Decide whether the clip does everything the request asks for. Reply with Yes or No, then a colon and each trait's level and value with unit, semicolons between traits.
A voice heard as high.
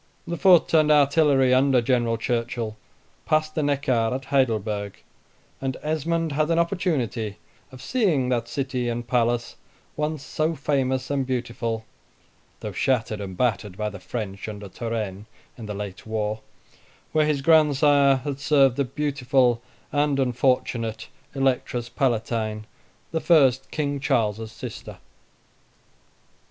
No: low, 130 Hz